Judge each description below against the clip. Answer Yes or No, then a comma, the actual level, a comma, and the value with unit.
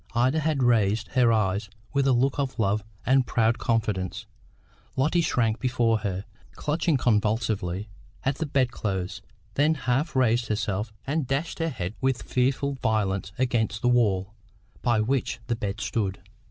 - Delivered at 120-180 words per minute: Yes, average, 155 wpm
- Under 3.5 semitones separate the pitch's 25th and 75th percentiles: No, average, 4.0 semitones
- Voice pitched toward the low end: Yes, low, 120 Hz